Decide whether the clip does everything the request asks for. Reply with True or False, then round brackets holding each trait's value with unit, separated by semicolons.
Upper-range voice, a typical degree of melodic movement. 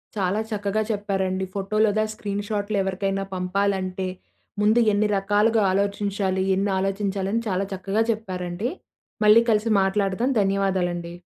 False (200 Hz; 1.7 semitones)